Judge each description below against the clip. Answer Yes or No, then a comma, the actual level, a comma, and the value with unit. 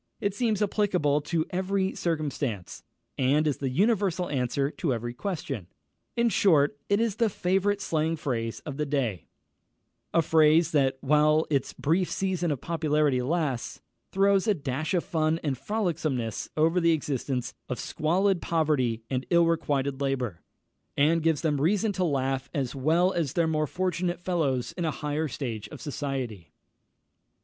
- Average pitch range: Yes, average, 4.7 semitones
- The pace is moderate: Yes, average, 155 wpm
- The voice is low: No, medium, 155 Hz